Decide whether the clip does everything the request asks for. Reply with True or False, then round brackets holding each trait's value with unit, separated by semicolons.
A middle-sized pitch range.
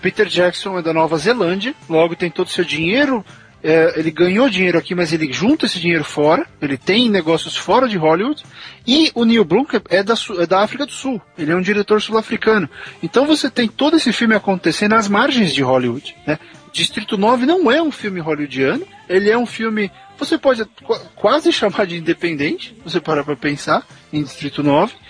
False (6.2 semitones)